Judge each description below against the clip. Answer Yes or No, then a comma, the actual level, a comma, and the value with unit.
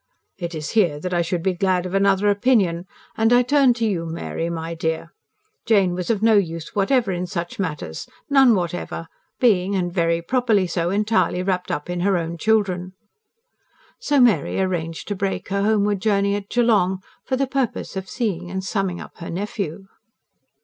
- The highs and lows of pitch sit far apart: No, average, 3.4 semitones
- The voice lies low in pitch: No, high, 190 Hz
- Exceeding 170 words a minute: Yes, average, 180 wpm